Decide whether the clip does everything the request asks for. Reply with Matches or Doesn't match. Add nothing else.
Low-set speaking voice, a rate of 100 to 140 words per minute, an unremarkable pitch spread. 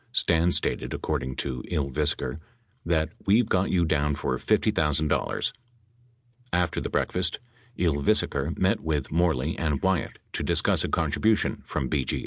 Matches